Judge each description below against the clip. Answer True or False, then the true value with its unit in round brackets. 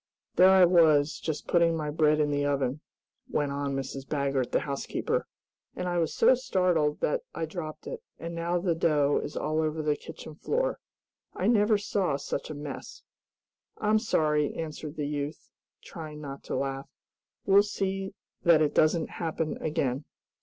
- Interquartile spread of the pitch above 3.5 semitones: False (3.2 semitones)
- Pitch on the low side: False (155 Hz)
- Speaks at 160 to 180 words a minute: True (165 wpm)